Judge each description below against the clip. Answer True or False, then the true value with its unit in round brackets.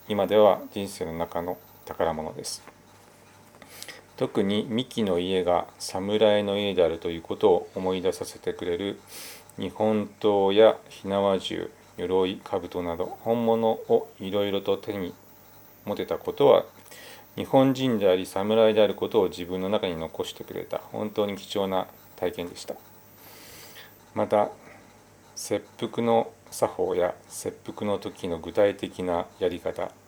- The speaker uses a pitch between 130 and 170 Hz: False (100 Hz)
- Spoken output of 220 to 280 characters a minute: True (245 characters per minute)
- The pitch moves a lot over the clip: False (3.3 semitones)